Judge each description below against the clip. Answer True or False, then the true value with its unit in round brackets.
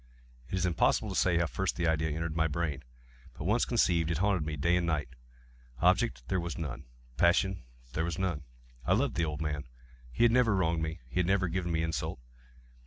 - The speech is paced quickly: True (210 wpm)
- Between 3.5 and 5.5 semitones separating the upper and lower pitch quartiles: False (3.0 semitones)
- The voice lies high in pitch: False (85 Hz)